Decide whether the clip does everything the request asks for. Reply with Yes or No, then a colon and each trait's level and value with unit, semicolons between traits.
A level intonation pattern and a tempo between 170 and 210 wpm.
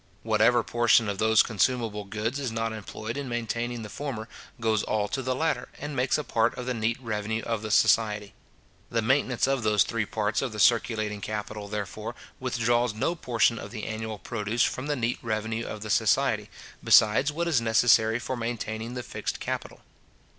Yes: narrow, 2.1 semitones; average, 185 wpm